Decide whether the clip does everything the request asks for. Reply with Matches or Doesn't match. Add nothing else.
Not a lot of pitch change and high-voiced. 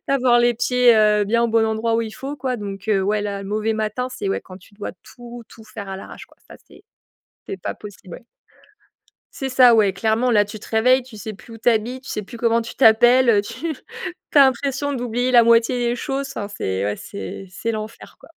Doesn't match